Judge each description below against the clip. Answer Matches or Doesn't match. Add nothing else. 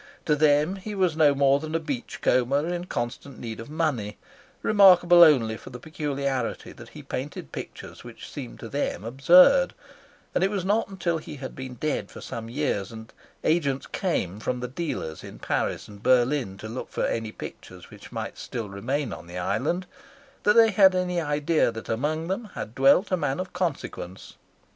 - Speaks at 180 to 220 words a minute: Matches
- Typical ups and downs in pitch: Doesn't match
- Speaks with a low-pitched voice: Doesn't match